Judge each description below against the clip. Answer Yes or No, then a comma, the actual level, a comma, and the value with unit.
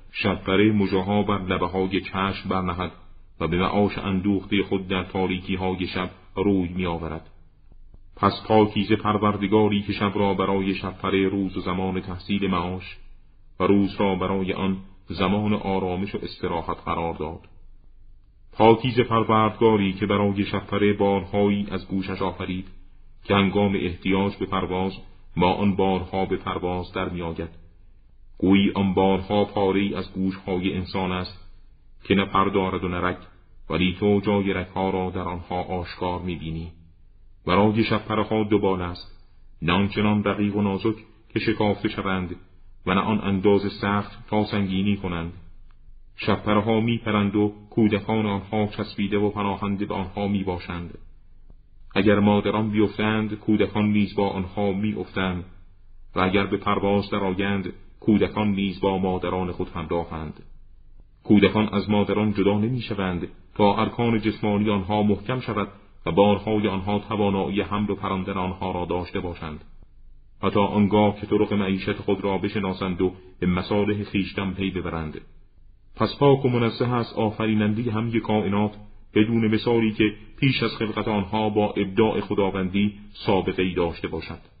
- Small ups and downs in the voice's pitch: Yes, narrow, 2.0 semitones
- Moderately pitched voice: No, low, 100 Hz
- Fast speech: No, average, 140 wpm